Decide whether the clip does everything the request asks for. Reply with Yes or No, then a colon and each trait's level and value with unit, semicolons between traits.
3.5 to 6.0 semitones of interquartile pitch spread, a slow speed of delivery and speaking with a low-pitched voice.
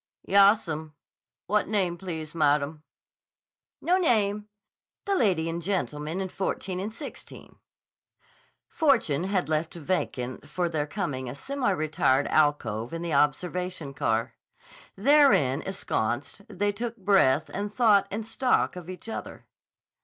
No: wide, 5.5 semitones; slow, 125 wpm; medium, 180 Hz